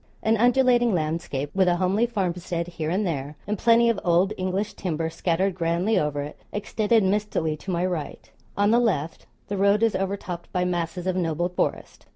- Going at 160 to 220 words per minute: Yes, average, 185 wpm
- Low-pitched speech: No, medium, 185 Hz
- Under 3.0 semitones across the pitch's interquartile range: No, average, 3.6 semitones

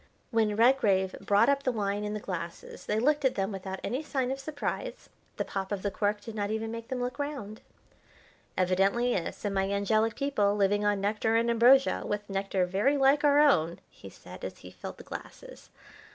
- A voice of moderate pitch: No, high, 215 Hz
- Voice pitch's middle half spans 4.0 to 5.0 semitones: Yes, average, 4.5 semitones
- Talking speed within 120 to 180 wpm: No, average, 195 wpm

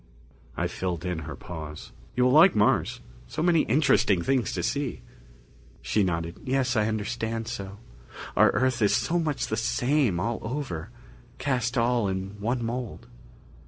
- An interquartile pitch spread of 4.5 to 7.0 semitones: Yes, average, 5.1 semitones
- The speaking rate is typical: Yes, average, 155 wpm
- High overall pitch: No, low, 115 Hz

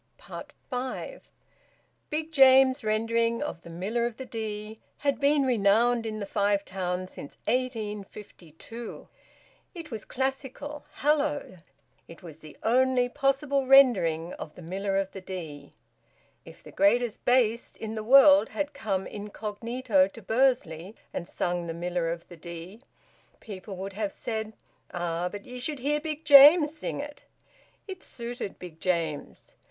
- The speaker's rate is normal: Yes, average, 145 wpm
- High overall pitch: Yes, high, 220 Hz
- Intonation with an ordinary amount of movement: No, wide, 6.0 semitones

